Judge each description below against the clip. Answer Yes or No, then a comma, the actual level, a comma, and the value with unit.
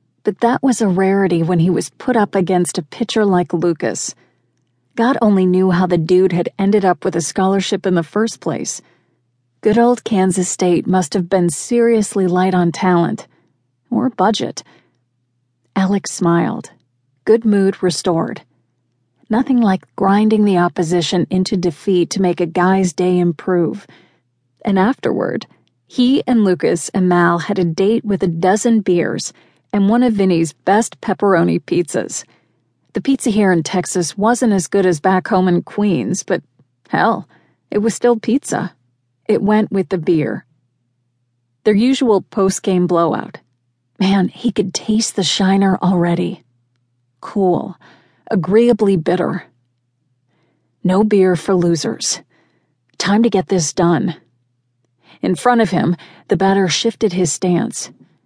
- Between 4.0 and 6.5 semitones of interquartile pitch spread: No, average, 3.5 semitones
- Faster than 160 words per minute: No, average, 145 wpm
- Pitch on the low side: No, medium, 185 Hz